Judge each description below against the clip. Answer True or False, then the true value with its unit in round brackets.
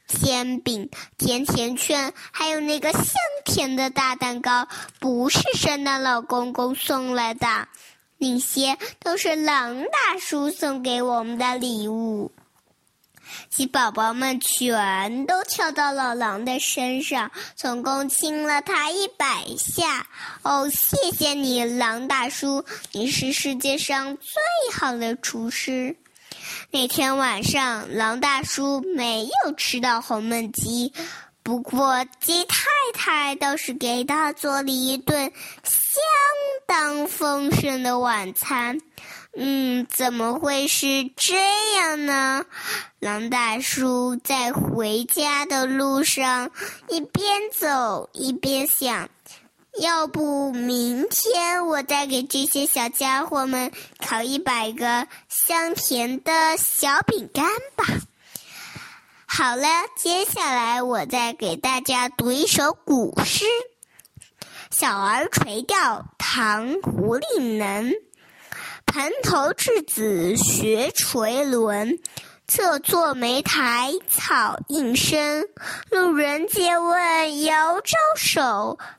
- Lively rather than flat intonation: False (4.0 semitones)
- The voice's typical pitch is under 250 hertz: False (275 Hz)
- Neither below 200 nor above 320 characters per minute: False (155 characters per minute)